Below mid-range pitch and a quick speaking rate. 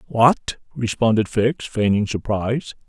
No: low, 110 Hz; slow, 105 wpm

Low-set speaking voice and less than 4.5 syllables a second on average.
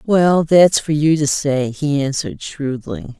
No: medium, 150 Hz; 3.9 syllables/s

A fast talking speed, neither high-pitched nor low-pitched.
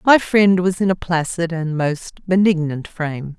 No: average, 175 wpm; medium, 175 Hz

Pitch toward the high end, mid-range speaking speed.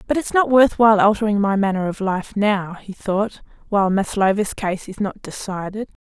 Yes: high, 205 Hz; average, 190 wpm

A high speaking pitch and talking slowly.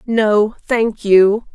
Yes: high, 215 Hz; slow, 115 wpm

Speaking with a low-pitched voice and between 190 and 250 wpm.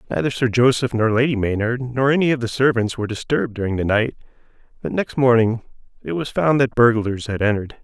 Yes: low, 120 Hz; average, 200 wpm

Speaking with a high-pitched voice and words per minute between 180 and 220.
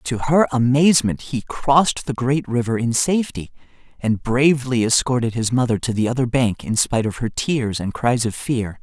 No: low, 120 Hz; average, 190 wpm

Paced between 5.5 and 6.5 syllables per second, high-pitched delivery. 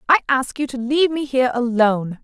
Yes: 6.2 syllables/s; very high, 255 Hz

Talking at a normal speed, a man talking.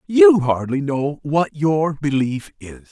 Yes: average, 145 wpm; male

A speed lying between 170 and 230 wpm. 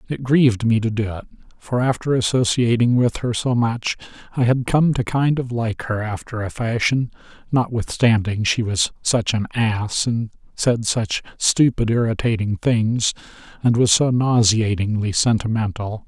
No: average, 155 wpm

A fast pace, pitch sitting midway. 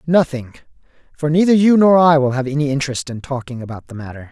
Yes: fast, 210 wpm; medium, 145 Hz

